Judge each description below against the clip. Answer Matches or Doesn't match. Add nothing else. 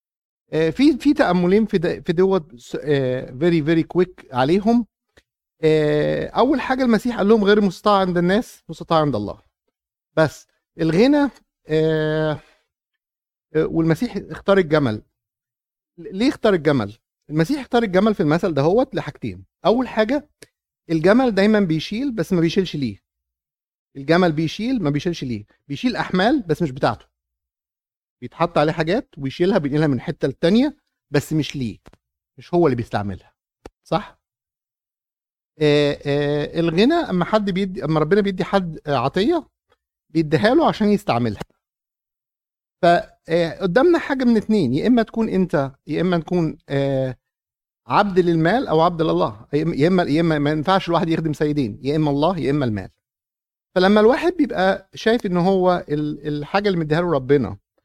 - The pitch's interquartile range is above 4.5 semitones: Matches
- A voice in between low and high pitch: Matches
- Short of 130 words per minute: Doesn't match